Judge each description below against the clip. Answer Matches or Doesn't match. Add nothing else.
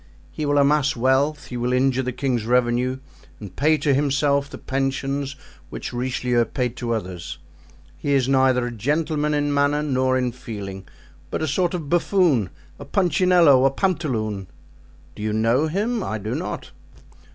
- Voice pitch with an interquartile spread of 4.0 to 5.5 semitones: Doesn't match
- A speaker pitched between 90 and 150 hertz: Matches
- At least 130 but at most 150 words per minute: Doesn't match